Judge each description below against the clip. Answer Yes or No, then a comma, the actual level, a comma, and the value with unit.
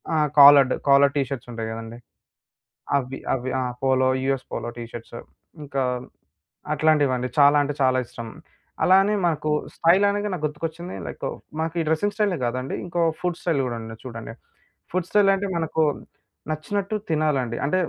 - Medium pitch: Yes, medium, 145 Hz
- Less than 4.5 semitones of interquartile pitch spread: No, average, 4.8 semitones